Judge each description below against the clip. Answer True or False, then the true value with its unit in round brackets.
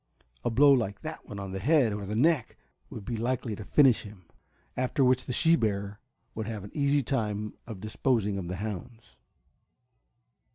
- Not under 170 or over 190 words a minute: True (175 wpm)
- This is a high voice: False (110 Hz)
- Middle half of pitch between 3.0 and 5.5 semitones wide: True (4.1 semitones)